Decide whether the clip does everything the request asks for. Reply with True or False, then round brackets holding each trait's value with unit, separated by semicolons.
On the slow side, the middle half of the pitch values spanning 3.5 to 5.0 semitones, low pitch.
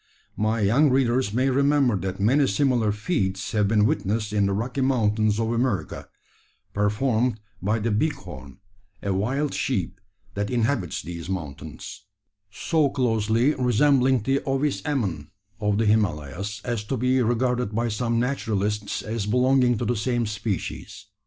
False (145 wpm; 3.9 semitones; 110 Hz)